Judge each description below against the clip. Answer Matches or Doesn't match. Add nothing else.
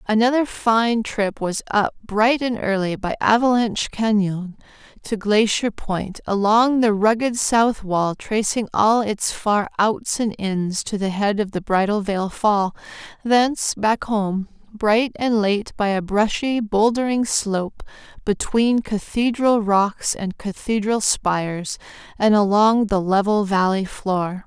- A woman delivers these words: Matches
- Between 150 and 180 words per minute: Doesn't match